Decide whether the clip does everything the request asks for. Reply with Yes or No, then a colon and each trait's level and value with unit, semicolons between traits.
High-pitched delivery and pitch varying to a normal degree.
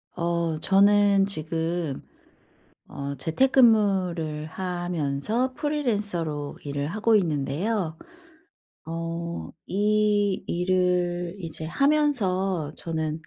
No: medium, 175 Hz; average, 4.4 semitones